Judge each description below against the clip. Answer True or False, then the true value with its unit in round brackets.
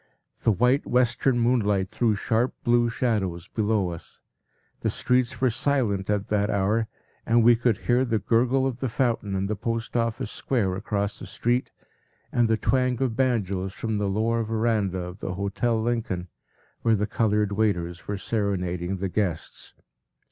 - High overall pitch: False (110 Hz)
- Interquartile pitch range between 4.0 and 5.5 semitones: False (3.2 semitones)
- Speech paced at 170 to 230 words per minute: False (160 wpm)